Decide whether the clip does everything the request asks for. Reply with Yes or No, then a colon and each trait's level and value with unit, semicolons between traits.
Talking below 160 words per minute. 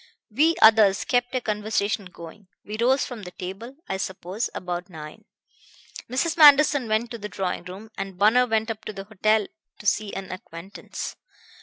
No: average, 170 wpm